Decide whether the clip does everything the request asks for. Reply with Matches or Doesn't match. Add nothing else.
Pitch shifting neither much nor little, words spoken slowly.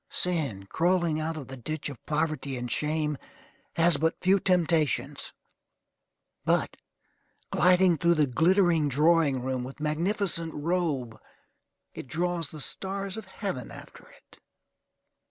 Matches